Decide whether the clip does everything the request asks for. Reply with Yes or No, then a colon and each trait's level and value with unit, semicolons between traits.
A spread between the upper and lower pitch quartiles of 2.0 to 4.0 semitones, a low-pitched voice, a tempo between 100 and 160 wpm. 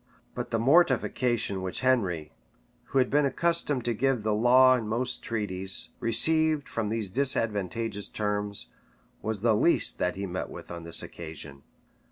No: average, 4.6 semitones; low, 115 Hz; average, 155 wpm